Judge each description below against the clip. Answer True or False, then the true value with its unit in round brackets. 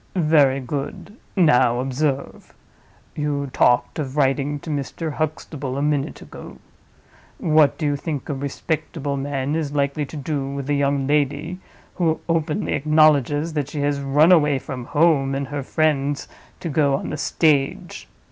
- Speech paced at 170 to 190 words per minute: False (155 wpm)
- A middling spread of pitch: False (2.0 semitones)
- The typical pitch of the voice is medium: True (145 Hz)